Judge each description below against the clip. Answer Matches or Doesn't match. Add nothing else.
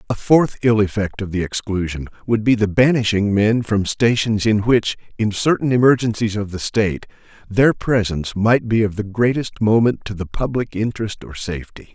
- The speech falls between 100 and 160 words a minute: Doesn't match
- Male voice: Matches